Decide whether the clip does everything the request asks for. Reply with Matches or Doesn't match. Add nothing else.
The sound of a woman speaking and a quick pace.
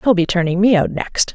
Matches